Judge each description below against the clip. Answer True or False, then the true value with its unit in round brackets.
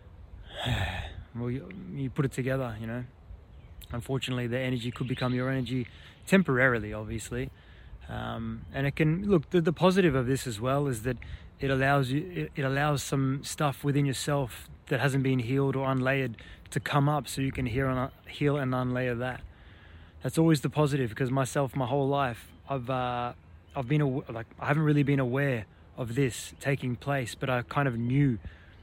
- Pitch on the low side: True (130 Hz)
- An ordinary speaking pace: True (185 wpm)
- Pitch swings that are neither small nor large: True (3.6 semitones)